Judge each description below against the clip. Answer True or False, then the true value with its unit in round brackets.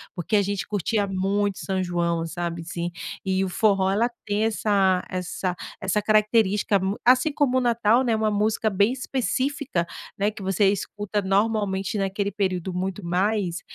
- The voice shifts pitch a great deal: False (2.5 semitones)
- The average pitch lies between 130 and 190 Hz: False (200 Hz)